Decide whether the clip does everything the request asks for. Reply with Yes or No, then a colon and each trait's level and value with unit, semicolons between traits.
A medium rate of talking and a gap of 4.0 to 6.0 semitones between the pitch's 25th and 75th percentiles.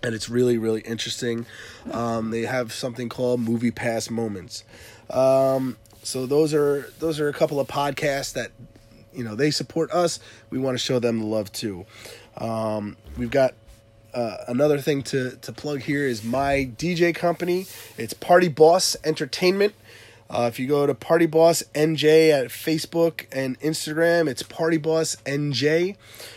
Yes: average, 160 wpm; average, 5.1 semitones